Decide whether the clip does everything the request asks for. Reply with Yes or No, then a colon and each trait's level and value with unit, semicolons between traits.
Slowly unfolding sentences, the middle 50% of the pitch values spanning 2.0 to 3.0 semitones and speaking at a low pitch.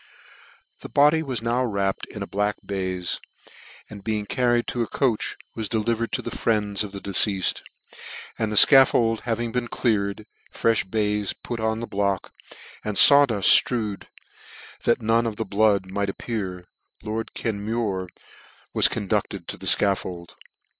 No: average, 155 wpm; average, 2.7 semitones; low, 110 Hz